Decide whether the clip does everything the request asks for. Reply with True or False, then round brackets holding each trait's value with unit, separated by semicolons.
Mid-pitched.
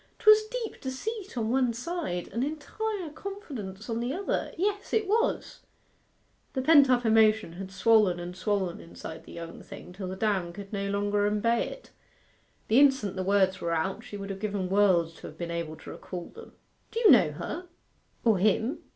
False (215 Hz)